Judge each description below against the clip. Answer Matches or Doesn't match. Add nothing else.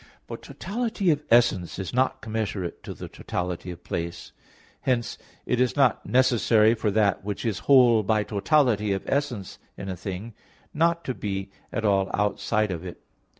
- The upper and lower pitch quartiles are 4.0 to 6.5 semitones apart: Matches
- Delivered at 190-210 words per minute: Doesn't match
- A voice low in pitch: Matches